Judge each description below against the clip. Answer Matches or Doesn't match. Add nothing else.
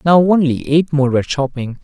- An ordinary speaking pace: Matches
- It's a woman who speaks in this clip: Doesn't match